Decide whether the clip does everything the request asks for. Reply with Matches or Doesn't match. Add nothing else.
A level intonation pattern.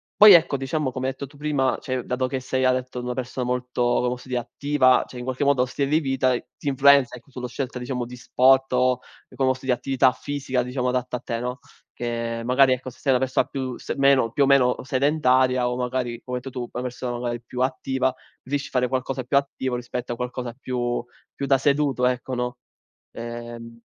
Matches